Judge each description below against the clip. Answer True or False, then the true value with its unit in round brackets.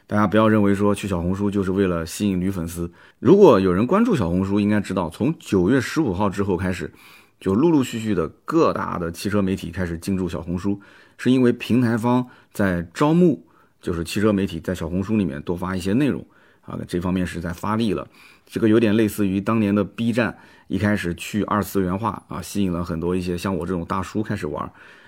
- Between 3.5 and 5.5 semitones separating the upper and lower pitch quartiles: False (3.0 semitones)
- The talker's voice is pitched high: False (100 Hz)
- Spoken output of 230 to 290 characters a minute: False (325 characters per minute)